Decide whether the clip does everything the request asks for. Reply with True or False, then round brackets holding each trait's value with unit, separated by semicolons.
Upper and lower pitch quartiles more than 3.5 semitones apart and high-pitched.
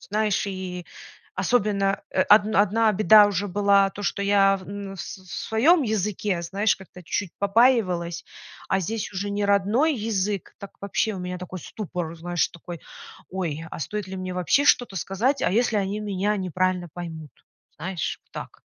False (2.5 semitones; 195 Hz)